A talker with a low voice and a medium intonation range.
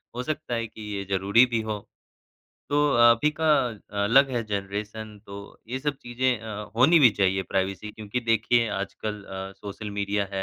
Yes: low, 110 Hz; average, 3.2 semitones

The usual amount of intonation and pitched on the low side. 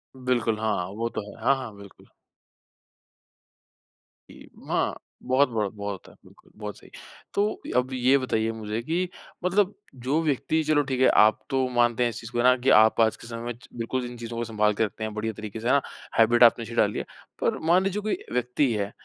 Yes: average, 3.1 semitones; low, 120 Hz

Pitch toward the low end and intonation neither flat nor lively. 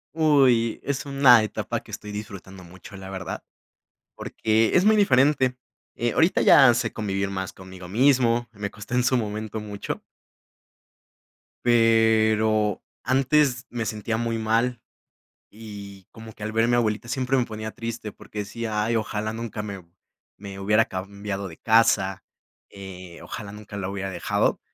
Yes: low, 110 Hz; average, 3.1 semitones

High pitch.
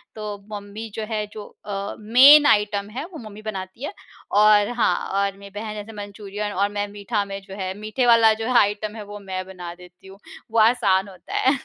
Yes: high, 205 Hz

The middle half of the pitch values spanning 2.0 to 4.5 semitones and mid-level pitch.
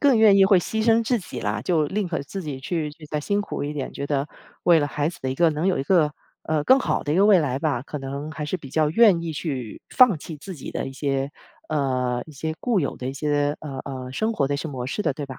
No: average, 5.0 semitones; medium, 150 Hz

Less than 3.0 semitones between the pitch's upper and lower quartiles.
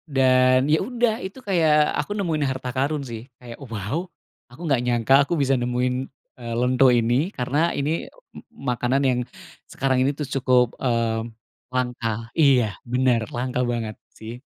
Yes: narrow, 2.4 semitones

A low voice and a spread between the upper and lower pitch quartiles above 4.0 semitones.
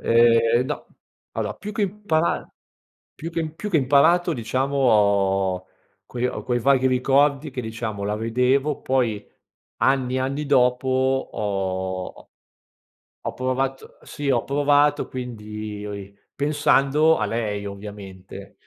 Yes: low, 125 Hz; average, 4.8 semitones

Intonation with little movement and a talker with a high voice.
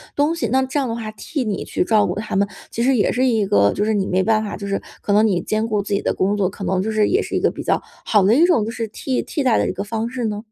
No: average, 3.1 semitones; high, 215 Hz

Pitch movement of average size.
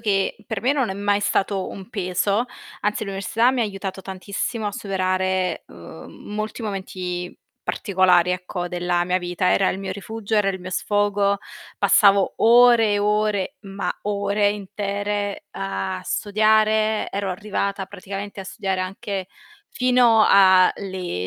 No: narrow, 2.0 semitones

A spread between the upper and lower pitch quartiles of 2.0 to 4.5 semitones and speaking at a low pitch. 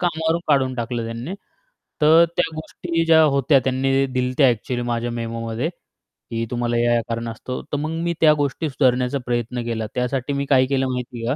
Yes: average, 3.4 semitones; low, 130 Hz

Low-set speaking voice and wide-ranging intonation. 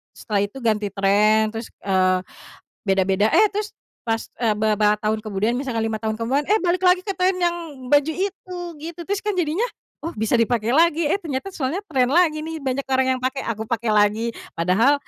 No: very high, 255 Hz; wide, 7.5 semitones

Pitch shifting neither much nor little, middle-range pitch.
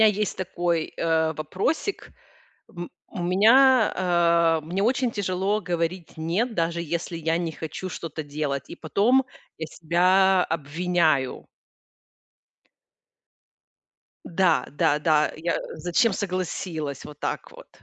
Yes: average, 3.0 semitones; medium, 170 Hz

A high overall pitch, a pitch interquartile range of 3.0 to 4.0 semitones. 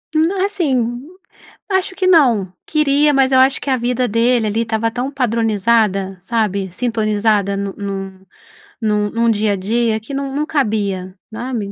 No: high, 230 Hz; average, 4.4 semitones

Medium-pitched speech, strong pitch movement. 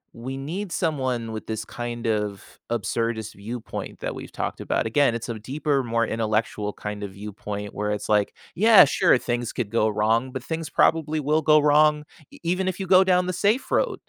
No: low, 120 Hz; wide, 6.0 semitones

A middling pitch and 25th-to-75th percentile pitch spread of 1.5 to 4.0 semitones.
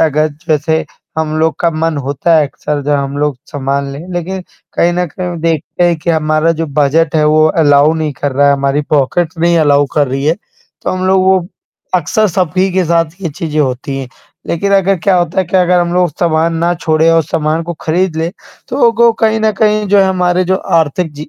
Yes: medium, 165 Hz; average, 3.2 semitones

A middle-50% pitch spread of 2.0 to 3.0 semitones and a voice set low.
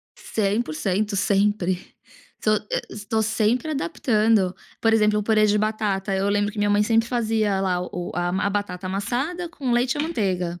No: average, 2.7 semitones; high, 210 Hz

